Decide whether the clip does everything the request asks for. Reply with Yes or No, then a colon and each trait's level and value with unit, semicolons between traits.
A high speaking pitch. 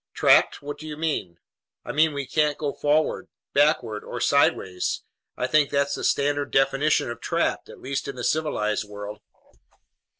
No: medium, 140 Hz